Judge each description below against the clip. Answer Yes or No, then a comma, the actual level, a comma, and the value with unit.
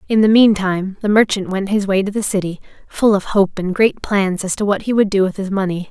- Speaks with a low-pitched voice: No, high, 200 Hz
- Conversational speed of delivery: No, fast, 265 wpm